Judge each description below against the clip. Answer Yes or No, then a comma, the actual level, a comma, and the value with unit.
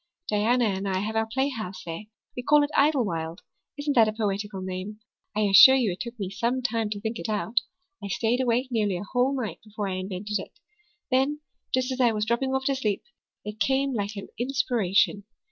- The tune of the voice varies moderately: Yes, average, 4.1 semitones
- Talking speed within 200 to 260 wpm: Yes, fast, 205 wpm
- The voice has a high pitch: Yes, high, 220 Hz